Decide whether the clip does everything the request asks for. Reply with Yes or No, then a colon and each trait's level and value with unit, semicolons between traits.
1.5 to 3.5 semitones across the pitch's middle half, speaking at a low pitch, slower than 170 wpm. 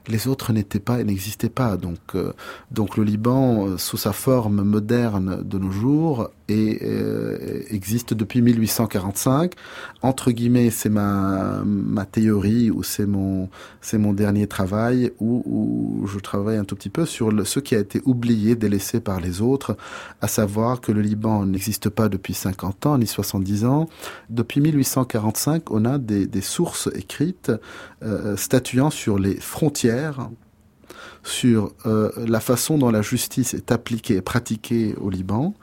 Yes: average, 3.1 semitones; low, 110 Hz; average, 160 wpm